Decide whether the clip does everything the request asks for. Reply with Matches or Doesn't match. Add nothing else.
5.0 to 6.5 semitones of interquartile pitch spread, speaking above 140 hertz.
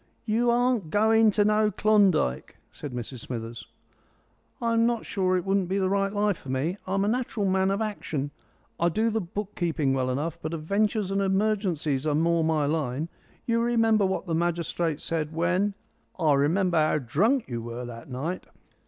Matches